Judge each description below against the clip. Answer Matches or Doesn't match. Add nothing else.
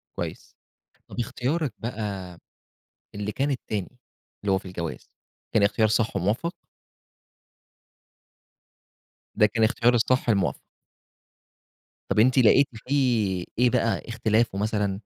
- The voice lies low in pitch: Matches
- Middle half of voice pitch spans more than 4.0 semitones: Doesn't match